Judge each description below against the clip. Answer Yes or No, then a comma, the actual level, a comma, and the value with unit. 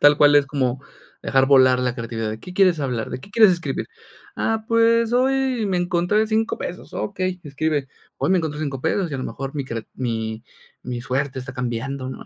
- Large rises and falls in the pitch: Yes, wide, 6.5 semitones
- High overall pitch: No, medium, 145 Hz